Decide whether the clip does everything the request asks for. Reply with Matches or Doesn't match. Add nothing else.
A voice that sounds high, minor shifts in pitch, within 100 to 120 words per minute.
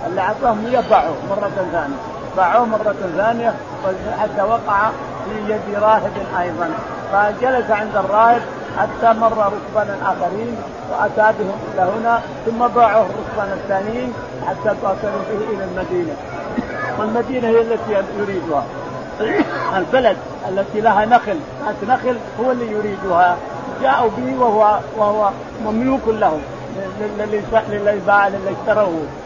Matches